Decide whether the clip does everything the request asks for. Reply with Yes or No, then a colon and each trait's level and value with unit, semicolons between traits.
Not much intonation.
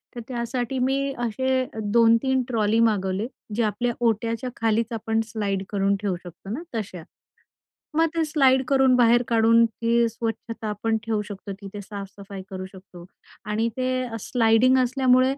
No: average, 3.2 semitones